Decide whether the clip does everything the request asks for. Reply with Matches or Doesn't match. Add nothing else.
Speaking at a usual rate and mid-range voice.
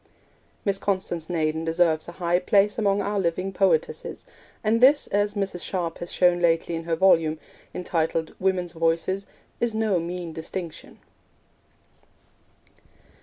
Doesn't match